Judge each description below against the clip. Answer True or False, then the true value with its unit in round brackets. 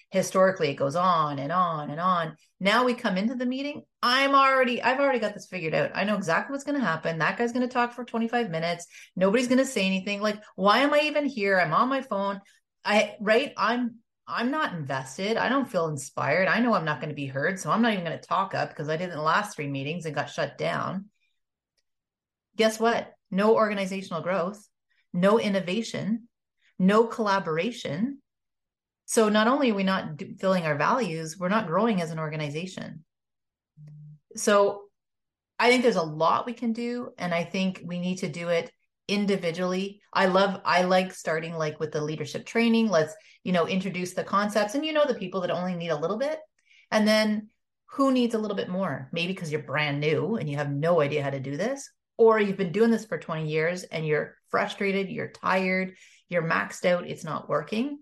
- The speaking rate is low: False (205 wpm)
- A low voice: False (195 Hz)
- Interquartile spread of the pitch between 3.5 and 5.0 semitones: False (5.5 semitones)